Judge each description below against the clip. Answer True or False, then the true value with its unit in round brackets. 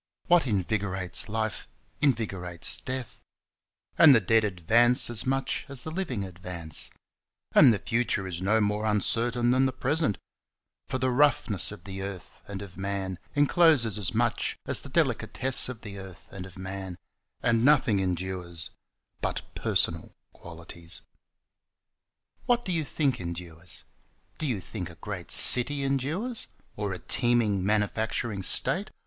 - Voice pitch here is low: True (105 Hz)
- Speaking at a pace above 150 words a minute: False (140 wpm)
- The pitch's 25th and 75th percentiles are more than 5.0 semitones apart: True (5.4 semitones)